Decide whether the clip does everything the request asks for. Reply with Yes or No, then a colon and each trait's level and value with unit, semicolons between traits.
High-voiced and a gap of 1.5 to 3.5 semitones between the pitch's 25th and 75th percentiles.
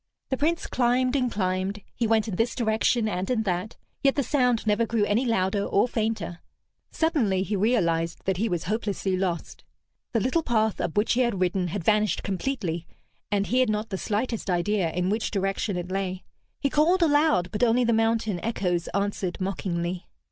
No: high, 210 Hz; average, 4.1 semitones